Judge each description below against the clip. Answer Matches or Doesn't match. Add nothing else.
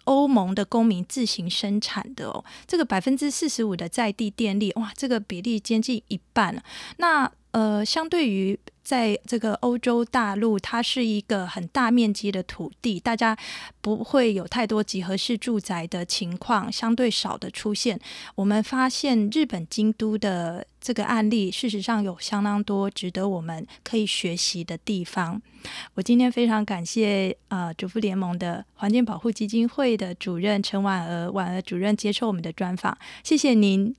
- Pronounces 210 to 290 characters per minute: Matches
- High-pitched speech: Matches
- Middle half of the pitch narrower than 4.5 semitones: Matches